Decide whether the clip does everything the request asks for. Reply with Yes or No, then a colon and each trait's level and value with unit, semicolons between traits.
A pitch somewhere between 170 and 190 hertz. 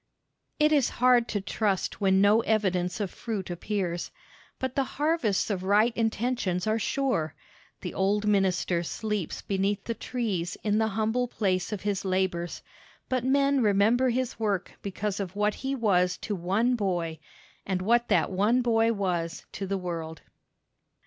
No: high, 205 Hz